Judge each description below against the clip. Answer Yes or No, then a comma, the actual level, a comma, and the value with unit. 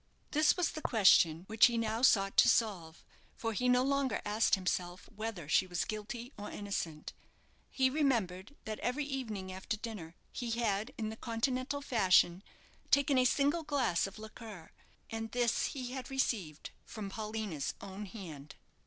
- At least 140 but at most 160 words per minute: Yes, average, 155 wpm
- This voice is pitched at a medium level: No, high, 220 Hz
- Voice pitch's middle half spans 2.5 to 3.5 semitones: No, average, 4.9 semitones